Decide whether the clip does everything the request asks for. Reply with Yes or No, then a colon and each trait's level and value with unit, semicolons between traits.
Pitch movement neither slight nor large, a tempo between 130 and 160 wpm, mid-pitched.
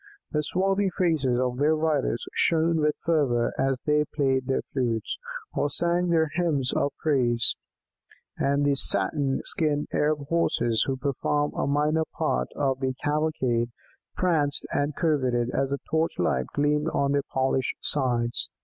Yes: average, 3.1 semitones; average, 150 wpm; medium, 145 Hz